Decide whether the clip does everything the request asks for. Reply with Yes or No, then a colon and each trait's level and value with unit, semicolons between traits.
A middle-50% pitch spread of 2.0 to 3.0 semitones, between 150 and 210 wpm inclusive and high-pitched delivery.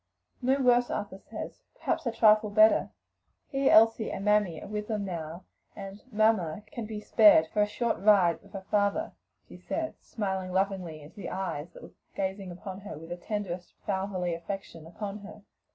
Yes: narrow, 2.6 semitones; average, 170 wpm; high, 200 Hz